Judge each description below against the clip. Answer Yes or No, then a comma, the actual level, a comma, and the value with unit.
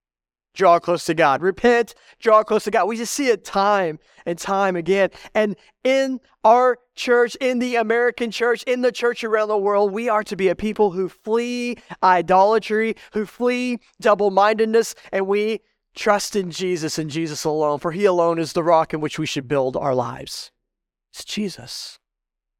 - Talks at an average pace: Yes, average, 180 wpm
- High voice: Yes, high, 205 Hz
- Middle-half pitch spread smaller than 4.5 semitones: No, average, 5.1 semitones